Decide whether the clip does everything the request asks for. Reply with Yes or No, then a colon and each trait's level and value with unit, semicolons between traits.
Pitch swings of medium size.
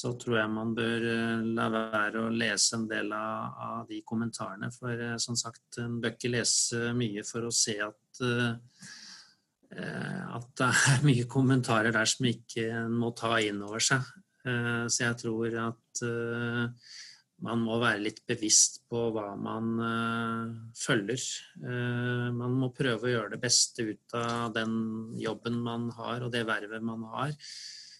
No: narrow, 1.3 semitones